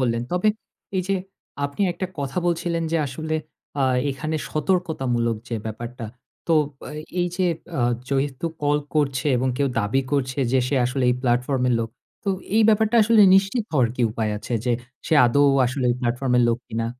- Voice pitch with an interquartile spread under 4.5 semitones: No, average, 5.3 semitones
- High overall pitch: No, low, 135 Hz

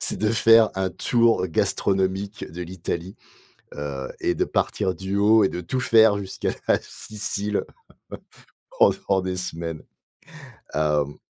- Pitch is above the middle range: No, very low, 95 Hz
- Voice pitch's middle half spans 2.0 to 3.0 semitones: No, average, 3.6 semitones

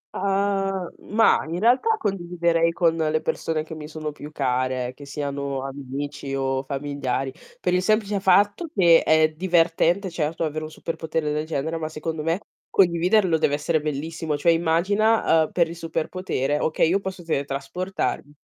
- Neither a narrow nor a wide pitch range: Yes, average, 3.8 semitones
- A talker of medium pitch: Yes, medium, 160 Hz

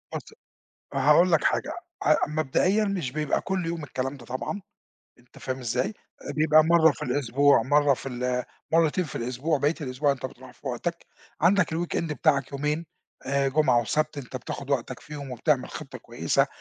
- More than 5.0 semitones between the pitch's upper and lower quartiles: No, average, 3.6 semitones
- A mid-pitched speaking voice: Yes, medium, 145 Hz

